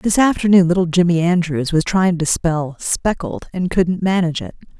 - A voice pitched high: No, medium, 175 Hz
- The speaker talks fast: No, average, 175 wpm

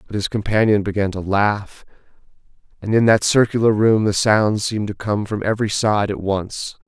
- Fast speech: No, average, 185 wpm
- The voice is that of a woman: No, male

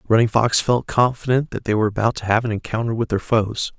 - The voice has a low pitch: Yes, low, 115 Hz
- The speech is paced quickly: Yes, fast, 240 wpm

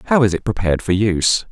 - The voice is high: No, low, 105 Hz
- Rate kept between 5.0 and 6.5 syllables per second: No, 7.0 syllables/s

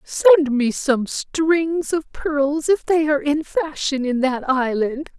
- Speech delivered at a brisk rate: No, average, 160 wpm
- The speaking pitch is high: Yes, very high, 290 Hz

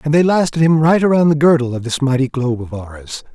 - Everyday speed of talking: No, fast, 250 wpm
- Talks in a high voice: No, medium, 140 Hz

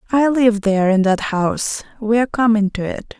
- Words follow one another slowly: No, fast, 205 wpm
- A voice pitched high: Yes, high, 215 Hz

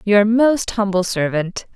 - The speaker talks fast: No, slow, 135 wpm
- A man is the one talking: No, female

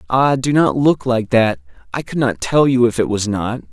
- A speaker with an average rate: No, fast, 240 wpm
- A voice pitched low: Yes, low, 120 Hz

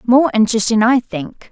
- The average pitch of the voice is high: Yes, high, 240 Hz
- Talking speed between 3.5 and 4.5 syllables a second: No, 5.2 syllables/s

